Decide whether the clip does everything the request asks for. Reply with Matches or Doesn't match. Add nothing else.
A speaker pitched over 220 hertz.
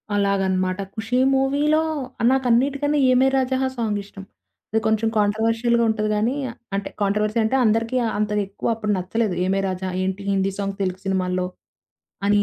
Doesn't match